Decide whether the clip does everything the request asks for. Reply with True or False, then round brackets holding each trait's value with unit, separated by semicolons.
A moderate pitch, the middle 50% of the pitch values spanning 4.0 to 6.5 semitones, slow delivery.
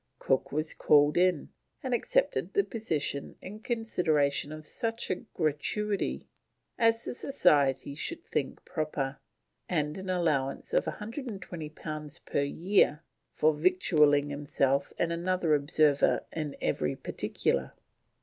True (155 Hz; 4.8 semitones; 120 wpm)